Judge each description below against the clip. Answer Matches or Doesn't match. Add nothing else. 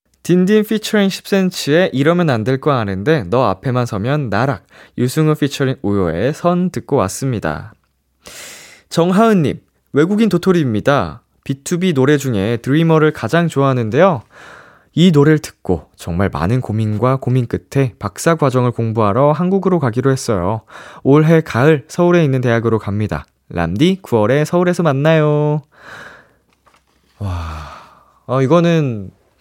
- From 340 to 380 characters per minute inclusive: Doesn't match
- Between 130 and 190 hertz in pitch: Matches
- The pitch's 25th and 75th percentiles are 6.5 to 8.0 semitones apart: Matches